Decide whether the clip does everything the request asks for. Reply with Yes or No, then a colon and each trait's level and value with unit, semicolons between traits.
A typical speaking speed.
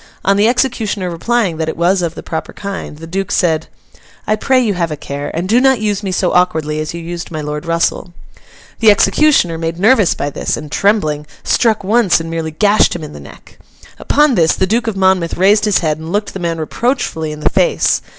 No: fast, 220 wpm